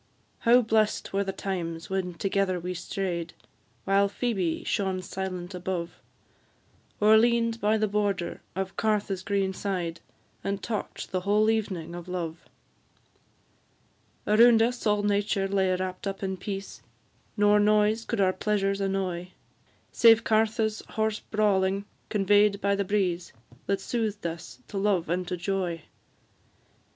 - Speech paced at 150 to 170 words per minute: No, slow, 135 wpm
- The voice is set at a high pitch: Yes, high, 195 Hz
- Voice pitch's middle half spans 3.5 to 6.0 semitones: No, narrow, 2.4 semitones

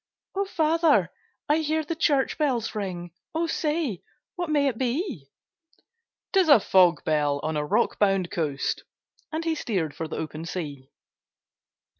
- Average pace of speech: Yes, average, 150 wpm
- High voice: Yes, high, 235 Hz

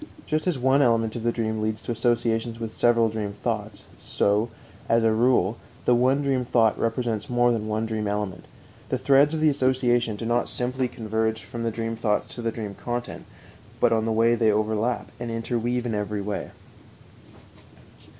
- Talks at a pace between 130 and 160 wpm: No, average, 185 wpm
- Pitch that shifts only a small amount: Yes, narrow, 1.9 semitones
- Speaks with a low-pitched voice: Yes, low, 115 Hz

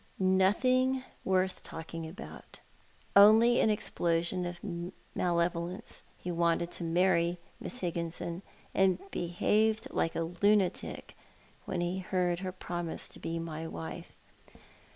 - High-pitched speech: No, medium, 175 Hz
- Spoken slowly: Yes, slow, 125 wpm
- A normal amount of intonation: No, narrow, 2.2 semitones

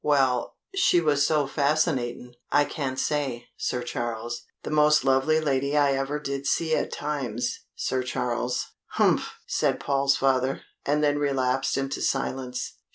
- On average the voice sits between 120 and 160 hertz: Yes, low, 135 Hz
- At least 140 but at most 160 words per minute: Yes, average, 145 wpm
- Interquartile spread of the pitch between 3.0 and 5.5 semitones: No, narrow, 2.5 semitones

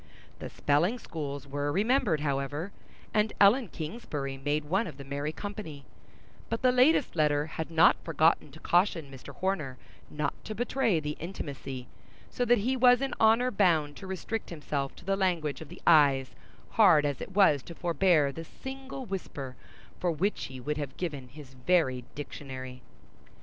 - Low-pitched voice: No, medium, 160 Hz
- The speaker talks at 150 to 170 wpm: Yes, average, 165 wpm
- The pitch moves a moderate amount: No, wide, 5.8 semitones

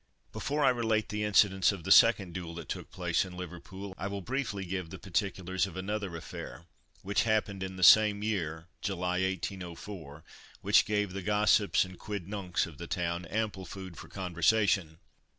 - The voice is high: No, very low, 95 Hz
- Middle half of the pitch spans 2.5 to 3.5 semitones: Yes, average, 2.8 semitones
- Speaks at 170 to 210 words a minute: Yes, average, 175 wpm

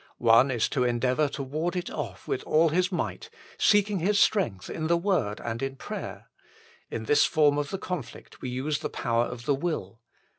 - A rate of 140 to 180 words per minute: No, average, 195 wpm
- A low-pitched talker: No, medium, 145 Hz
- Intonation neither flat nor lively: No, wide, 6.0 semitones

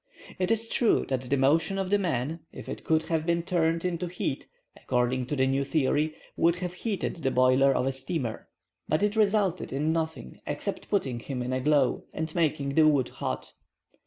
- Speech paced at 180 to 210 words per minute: Yes, average, 195 wpm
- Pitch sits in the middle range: Yes, medium, 155 Hz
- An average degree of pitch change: Yes, average, 4.7 semitones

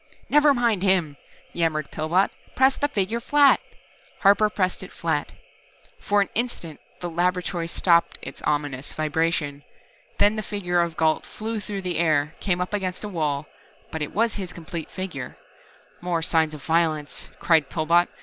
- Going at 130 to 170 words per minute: Yes, average, 160 wpm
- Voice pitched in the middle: Yes, medium, 175 Hz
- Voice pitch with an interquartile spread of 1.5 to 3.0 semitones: No, average, 4.3 semitones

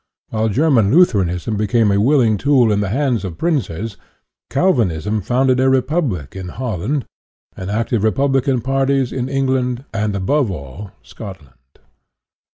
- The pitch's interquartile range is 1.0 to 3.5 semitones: No, average, 5.2 semitones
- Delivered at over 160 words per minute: No, average, 145 wpm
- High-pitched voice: No, low, 115 Hz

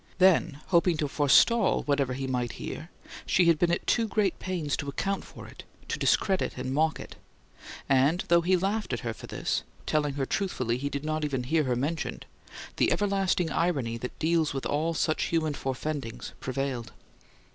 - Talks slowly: No, average, 180 wpm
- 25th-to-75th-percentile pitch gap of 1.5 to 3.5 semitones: No, average, 4.5 semitones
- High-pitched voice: No, medium, 150 Hz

